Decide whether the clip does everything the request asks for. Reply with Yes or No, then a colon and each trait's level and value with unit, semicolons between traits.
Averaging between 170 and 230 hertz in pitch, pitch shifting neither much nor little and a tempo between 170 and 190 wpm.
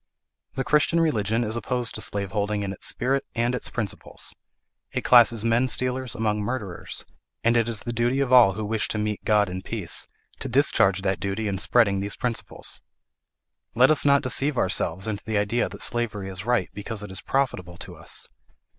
No: low, 110 Hz; average, 3.4 semitones; average, 185 wpm